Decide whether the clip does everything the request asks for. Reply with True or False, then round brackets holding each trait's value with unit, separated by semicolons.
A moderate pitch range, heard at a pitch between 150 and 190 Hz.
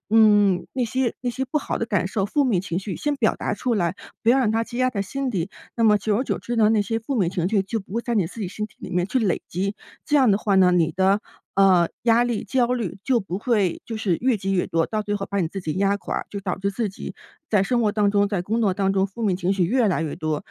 False (3.4 semitones; 205 Hz)